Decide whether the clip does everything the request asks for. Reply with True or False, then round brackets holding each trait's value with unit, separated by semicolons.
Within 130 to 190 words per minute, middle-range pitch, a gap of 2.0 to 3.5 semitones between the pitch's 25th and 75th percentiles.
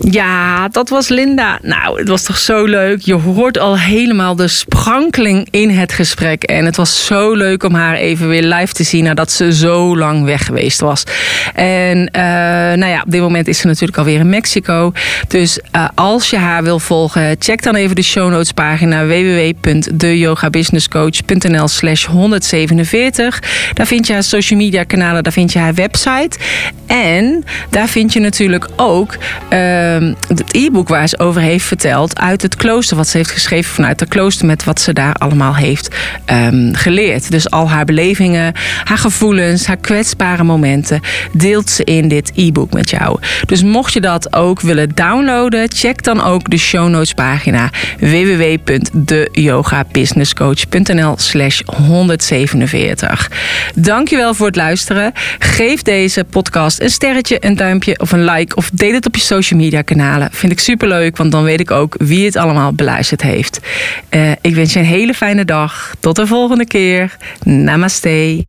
False (170 wpm; 175 Hz; 4.0 semitones)